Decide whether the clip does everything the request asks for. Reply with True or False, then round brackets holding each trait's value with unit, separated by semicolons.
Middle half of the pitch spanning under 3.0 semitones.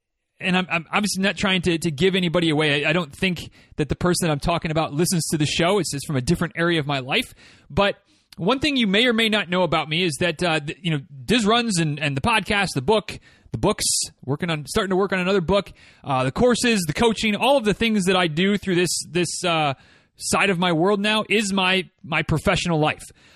False (4.1 semitones)